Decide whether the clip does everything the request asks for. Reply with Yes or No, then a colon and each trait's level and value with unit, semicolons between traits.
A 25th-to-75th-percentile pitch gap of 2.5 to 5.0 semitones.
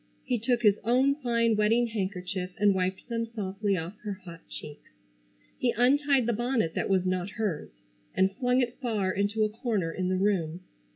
Yes: average, 4.2 semitones